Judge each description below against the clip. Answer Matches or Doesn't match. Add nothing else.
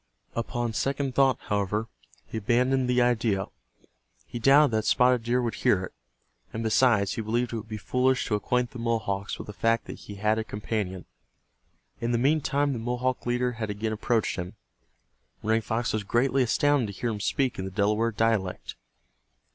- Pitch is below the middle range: Matches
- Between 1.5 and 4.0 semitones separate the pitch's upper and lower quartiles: Matches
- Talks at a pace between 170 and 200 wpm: Matches